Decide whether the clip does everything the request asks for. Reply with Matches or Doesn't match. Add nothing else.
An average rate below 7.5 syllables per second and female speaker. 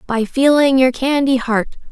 Matches